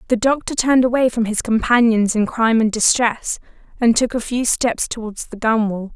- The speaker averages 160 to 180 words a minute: No, average, 190 wpm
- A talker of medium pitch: No, high, 230 Hz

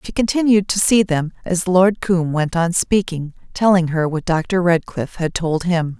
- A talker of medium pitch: Yes, medium, 175 Hz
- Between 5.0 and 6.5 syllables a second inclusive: No, 4.5 syllables/s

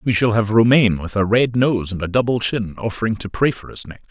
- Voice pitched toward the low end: Yes, low, 110 Hz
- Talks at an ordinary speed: No, fast, 265 wpm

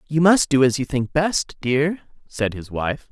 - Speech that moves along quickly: Yes, fast, 210 wpm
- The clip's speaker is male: Yes, male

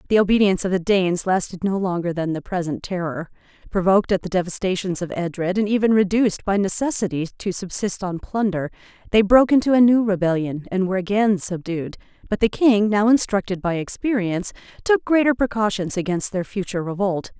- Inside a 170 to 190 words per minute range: Yes, average, 175 wpm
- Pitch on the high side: Yes, high, 195 Hz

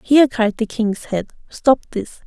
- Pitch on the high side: Yes, high, 230 Hz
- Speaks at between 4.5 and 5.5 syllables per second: No, 4.3 syllables/s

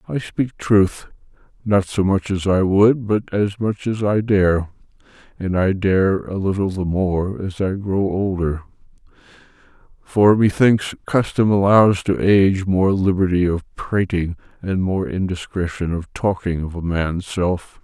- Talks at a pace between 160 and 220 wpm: No, average, 150 wpm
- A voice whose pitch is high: No, very low, 95 Hz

